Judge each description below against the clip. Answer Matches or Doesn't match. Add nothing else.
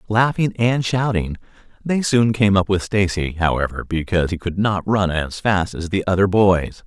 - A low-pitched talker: Matches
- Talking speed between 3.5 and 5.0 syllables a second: Matches